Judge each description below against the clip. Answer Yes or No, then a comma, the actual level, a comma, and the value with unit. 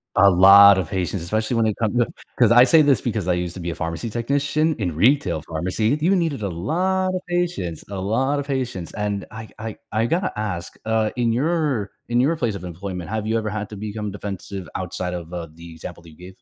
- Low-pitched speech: Yes, low, 105 Hz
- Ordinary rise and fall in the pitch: No, wide, 5.7 semitones